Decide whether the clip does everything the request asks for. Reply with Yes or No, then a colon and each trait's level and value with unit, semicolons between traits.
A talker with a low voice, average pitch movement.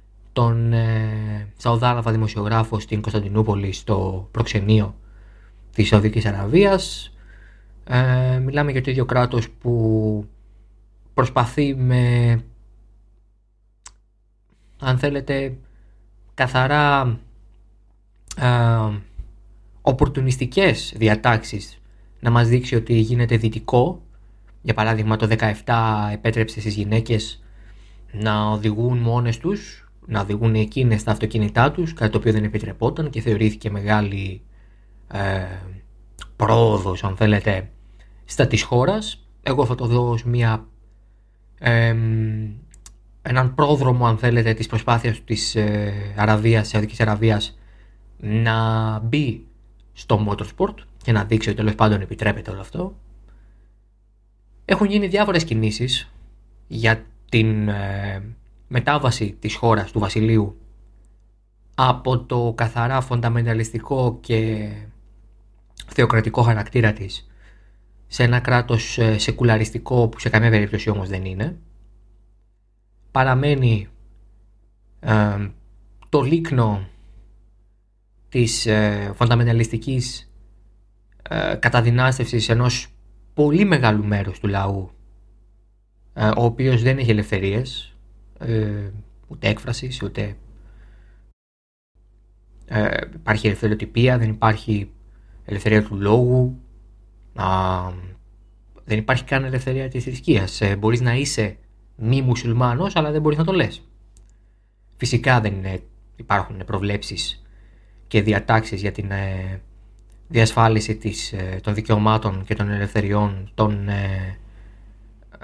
No: low, 110 Hz; narrow, 2.1 semitones